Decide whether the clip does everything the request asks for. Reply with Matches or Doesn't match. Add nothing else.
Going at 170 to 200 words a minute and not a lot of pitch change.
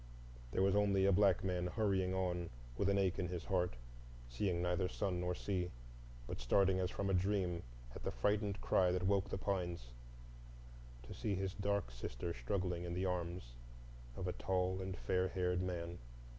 Matches